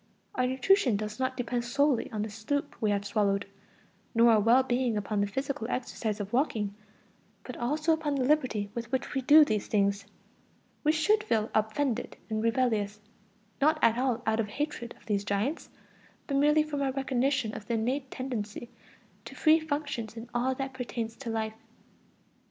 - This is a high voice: Yes, high, 240 Hz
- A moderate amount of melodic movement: Yes, average, 4.1 semitones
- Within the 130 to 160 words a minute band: No, average, 175 wpm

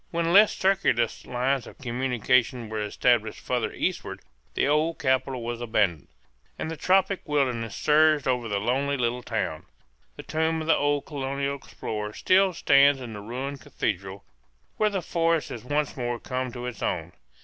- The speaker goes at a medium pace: Yes, average, 165 wpm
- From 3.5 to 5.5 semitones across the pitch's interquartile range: Yes, average, 4.4 semitones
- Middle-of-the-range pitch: No, low, 130 Hz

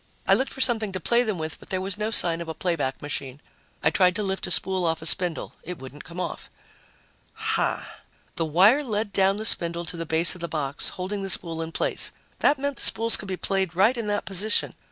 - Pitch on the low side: No, medium, 185 Hz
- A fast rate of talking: Yes, fast, 235 wpm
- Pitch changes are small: No, average, 4.2 semitones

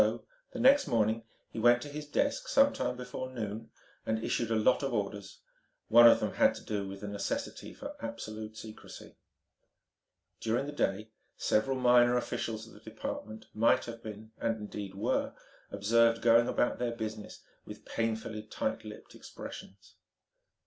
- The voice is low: Yes, low, 115 Hz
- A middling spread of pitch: No, narrow, 2.2 semitones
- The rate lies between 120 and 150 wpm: No, average, 165 wpm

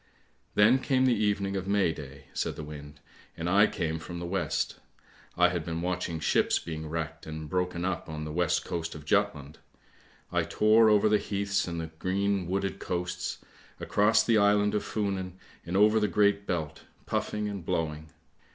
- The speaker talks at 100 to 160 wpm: No, average, 180 wpm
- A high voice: No, very low, 90 Hz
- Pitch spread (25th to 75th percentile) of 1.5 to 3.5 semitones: No, average, 4.2 semitones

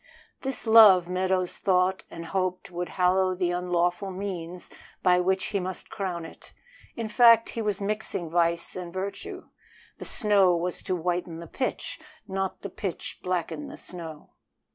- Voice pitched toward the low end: No, medium, 185 Hz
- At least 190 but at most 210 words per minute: No, average, 155 wpm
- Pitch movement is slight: Yes, narrow, 2.1 semitones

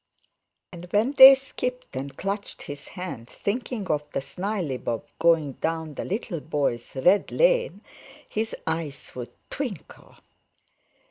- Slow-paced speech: Yes, slow, 125 wpm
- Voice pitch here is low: No, medium, 175 Hz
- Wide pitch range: Yes, wide, 7.2 semitones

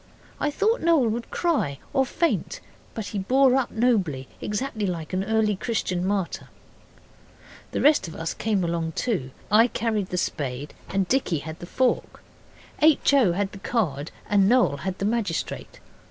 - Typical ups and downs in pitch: No, wide, 6.1 semitones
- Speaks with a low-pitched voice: No, high, 205 Hz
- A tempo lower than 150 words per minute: No, average, 165 wpm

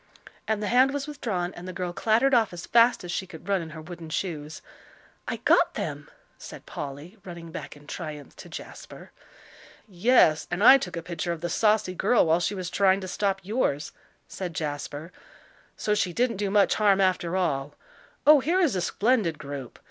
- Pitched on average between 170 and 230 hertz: Yes, medium, 185 Hz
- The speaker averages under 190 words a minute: No, average, 195 wpm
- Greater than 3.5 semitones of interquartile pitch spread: Yes, average, 4.3 semitones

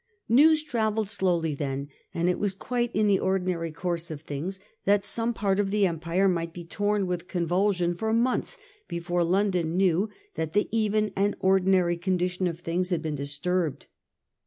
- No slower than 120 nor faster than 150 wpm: No, average, 175 wpm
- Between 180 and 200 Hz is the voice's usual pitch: Yes, medium, 185 Hz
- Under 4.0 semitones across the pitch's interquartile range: Yes, average, 3.2 semitones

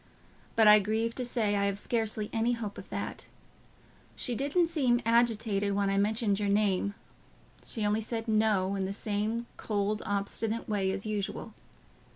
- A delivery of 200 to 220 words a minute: No, average, 165 wpm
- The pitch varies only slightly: Yes, narrow, 2.3 semitones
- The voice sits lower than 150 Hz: No, high, 215 Hz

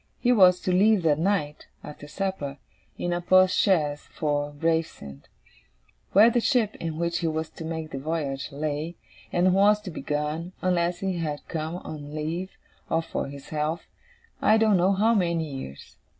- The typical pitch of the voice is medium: Yes, medium, 165 Hz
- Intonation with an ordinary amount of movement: Yes, average, 3.8 semitones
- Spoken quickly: No, average, 175 wpm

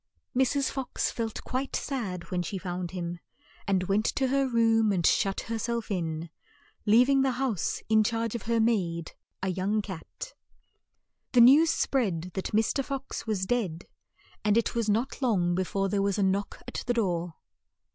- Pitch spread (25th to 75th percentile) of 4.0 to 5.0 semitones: Yes, average, 4.6 semitones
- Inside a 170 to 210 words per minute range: Yes, average, 175 wpm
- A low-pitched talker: No, high, 215 Hz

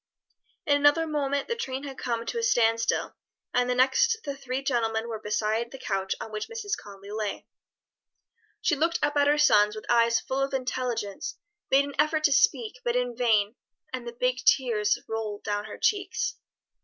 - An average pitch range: Yes, average, 4.3 semitones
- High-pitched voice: Yes, very high, 250 Hz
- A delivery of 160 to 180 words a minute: No, average, 190 wpm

